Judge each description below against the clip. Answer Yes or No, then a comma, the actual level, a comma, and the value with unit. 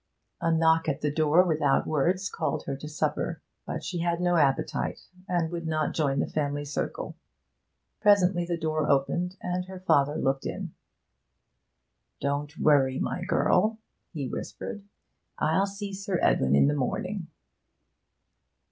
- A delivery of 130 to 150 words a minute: Yes, average, 145 wpm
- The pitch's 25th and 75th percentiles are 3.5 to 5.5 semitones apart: Yes, average, 3.8 semitones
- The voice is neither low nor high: Yes, medium, 160 Hz